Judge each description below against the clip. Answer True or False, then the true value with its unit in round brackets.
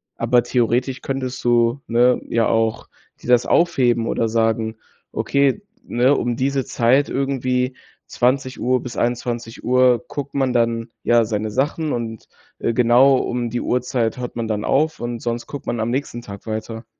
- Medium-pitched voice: False (120 Hz)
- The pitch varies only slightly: True (1.8 semitones)